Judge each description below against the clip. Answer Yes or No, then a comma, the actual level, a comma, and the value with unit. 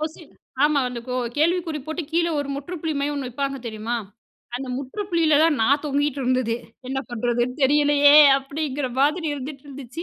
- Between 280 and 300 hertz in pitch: Yes, very high, 285 Hz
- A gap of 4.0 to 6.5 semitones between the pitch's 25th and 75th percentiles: No, average, 3.0 semitones